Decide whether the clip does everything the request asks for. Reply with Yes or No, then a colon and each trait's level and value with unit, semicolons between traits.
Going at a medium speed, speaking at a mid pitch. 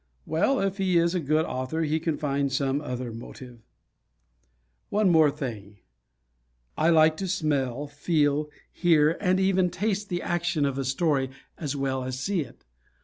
Yes: average, 160 wpm; medium, 155 Hz